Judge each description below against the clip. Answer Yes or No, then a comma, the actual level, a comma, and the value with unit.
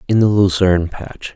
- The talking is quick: No, average, 175 wpm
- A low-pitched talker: Yes, very low, 95 Hz